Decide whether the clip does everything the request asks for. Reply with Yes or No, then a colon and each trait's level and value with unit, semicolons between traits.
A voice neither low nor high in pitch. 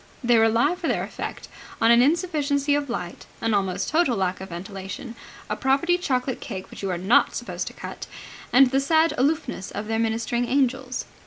No: high, 245 Hz